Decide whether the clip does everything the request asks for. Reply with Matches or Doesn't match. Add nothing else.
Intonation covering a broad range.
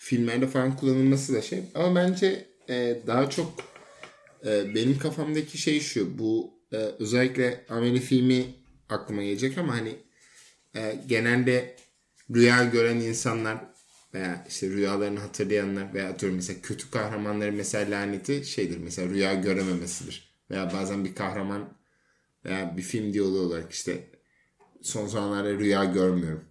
Doesn't match